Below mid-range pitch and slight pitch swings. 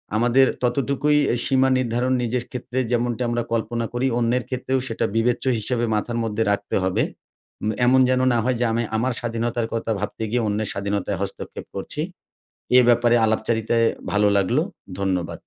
Yes: low, 120 Hz; narrow, 2.1 semitones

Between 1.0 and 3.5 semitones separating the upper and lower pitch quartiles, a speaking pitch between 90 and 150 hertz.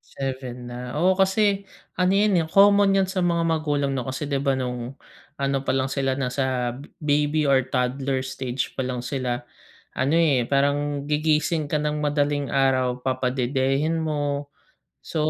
Yes: average, 3.0 semitones; medium, 140 Hz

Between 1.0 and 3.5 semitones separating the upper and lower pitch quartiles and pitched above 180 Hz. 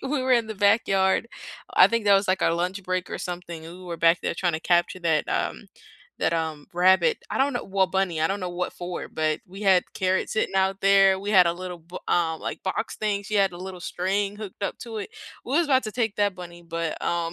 Yes: average, 2.7 semitones; high, 190 Hz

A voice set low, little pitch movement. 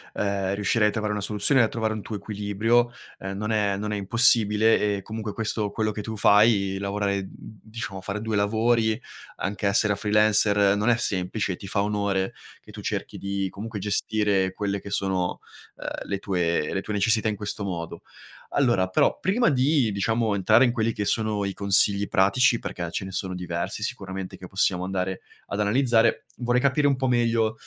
Yes: low, 105 Hz; narrow, 2.3 semitones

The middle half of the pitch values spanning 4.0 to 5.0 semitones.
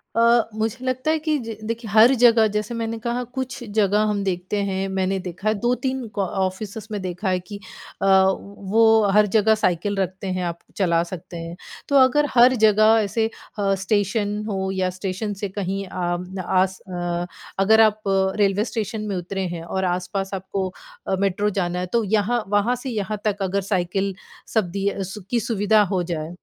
No: average, 2.8 semitones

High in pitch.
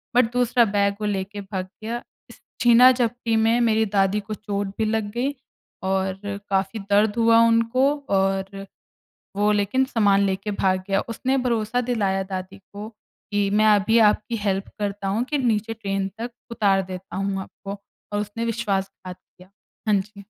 Yes: high, 205 Hz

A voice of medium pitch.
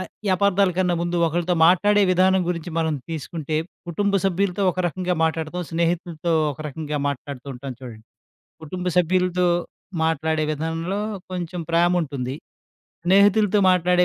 Yes: medium, 175 Hz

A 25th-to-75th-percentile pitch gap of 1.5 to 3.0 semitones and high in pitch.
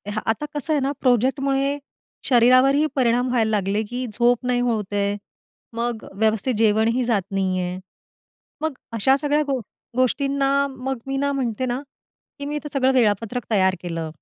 No: average, 3.9 semitones; high, 245 Hz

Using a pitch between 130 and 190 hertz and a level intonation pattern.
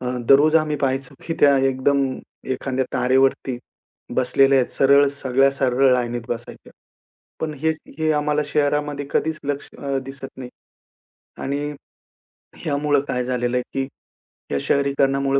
Yes: low, 135 Hz; narrow, 1.7 semitones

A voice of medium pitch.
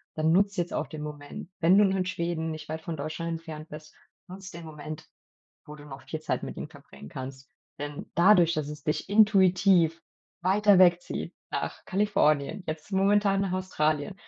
Yes: medium, 165 Hz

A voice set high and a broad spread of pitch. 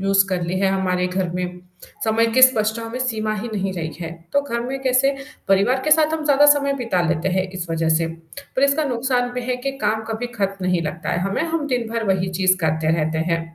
Yes: high, 215 Hz; wide, 5.9 semitones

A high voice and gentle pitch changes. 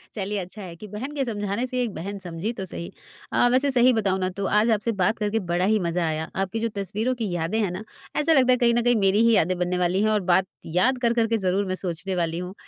No: high, 205 Hz; average, 4.2 semitones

